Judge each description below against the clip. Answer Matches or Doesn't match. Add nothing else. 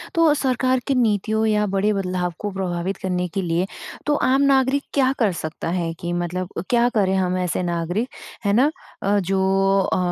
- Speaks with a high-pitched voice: Matches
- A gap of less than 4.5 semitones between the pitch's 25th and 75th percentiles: Doesn't match